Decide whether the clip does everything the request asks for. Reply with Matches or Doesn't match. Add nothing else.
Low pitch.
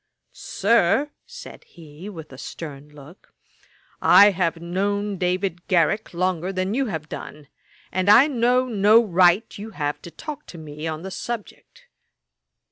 Doesn't match